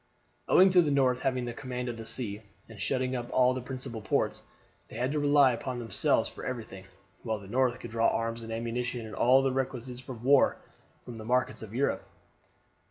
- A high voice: No, low, 125 Hz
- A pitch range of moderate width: No, narrow, 2.3 semitones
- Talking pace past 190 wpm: Yes, fast, 205 wpm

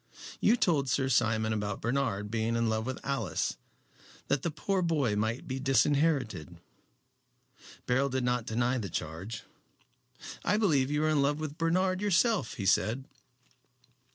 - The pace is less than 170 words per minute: Yes, average, 150 wpm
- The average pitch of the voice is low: Yes, low, 130 Hz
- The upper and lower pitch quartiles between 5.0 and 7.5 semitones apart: Yes, wide, 5.6 semitones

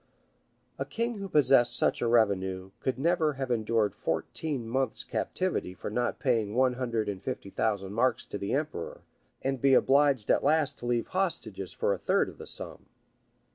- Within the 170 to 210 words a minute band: Yes, average, 175 wpm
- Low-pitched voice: Yes, low, 120 Hz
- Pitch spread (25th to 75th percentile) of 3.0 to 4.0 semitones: No, average, 5.3 semitones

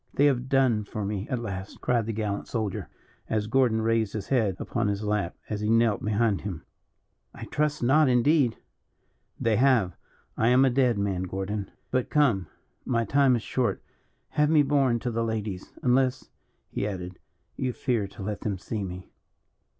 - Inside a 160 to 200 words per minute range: Yes, average, 175 wpm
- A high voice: No, low, 115 Hz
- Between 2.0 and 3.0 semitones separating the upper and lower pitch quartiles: No, average, 3.9 semitones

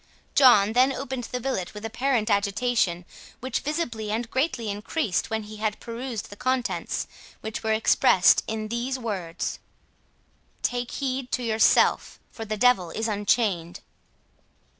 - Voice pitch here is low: No, high, 225 Hz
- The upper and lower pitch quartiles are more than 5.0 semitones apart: No, average, 3.1 semitones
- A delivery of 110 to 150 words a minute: Yes, average, 140 wpm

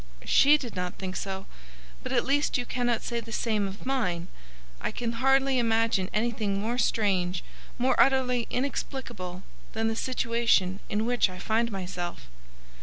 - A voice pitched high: Yes, high, 225 Hz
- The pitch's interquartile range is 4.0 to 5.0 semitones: Yes, average, 4.3 semitones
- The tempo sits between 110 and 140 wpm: No, average, 155 wpm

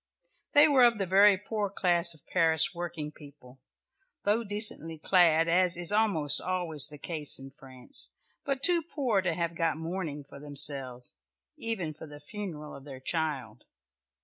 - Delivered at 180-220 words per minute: No, average, 160 wpm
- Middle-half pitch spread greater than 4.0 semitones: Yes, average, 5.1 semitones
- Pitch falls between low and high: Yes, medium, 170 Hz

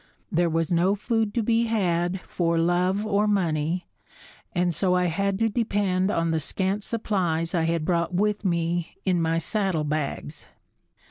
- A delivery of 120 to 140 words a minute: No, average, 155 wpm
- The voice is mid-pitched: Yes, medium, 180 Hz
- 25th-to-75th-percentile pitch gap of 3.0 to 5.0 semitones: Yes, average, 3.4 semitones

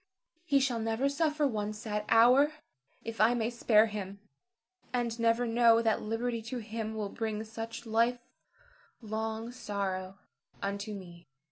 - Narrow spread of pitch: Yes, narrow, 2.1 semitones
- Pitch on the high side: Yes, high, 225 Hz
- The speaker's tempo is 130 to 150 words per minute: Yes, average, 140 wpm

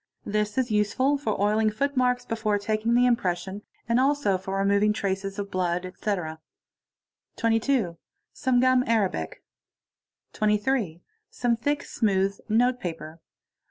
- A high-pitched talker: Yes, high, 210 Hz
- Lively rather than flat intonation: No, average, 4.1 semitones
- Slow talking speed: Yes, slow, 115 wpm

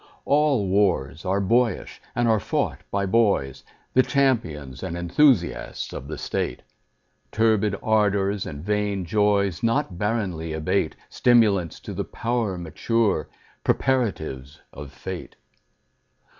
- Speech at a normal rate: No, slow, 115 wpm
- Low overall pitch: Yes, low, 100 Hz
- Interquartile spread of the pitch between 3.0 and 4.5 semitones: No, average, 5.1 semitones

